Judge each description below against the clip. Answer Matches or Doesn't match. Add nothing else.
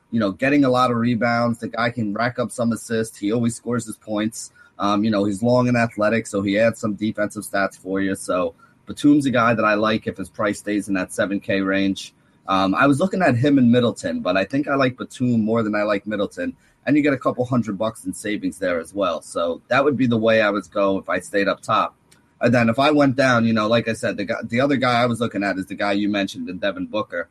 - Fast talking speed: Matches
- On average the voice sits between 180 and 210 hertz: Doesn't match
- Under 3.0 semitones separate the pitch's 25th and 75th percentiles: Doesn't match